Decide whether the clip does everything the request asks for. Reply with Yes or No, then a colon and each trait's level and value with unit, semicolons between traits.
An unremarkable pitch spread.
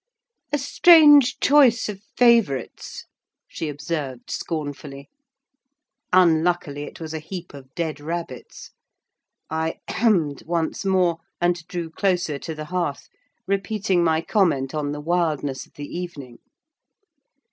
Yes: average, 4.2 semitones